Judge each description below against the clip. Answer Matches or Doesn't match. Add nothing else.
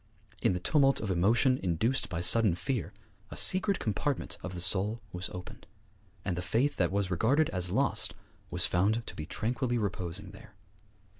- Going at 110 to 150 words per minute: Doesn't match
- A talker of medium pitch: Doesn't match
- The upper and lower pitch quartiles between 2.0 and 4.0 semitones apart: Doesn't match